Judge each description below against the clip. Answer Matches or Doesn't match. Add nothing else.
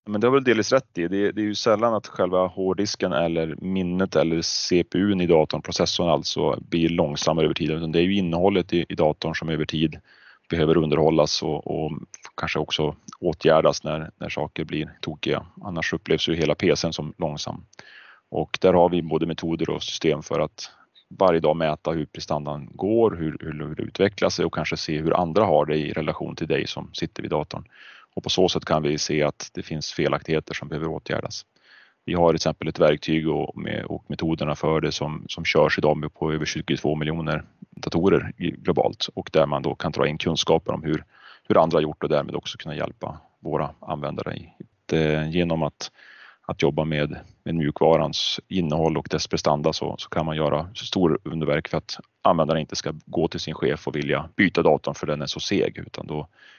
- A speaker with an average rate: Doesn't match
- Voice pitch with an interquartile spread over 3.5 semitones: Doesn't match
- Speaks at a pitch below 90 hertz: Matches